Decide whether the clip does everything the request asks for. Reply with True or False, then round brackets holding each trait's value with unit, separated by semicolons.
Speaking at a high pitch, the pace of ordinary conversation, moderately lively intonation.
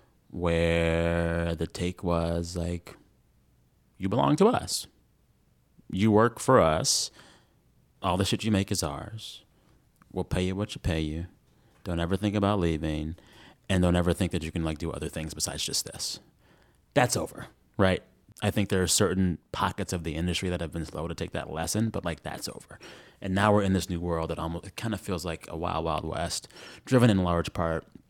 False (85 Hz; 195 wpm; 3.1 semitones)